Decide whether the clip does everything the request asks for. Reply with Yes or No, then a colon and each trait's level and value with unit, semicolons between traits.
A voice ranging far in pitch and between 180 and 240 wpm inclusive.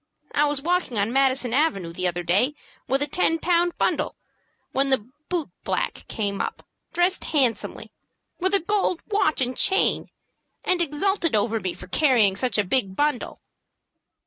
No: wide, 7.6 semitones; average, 160 wpm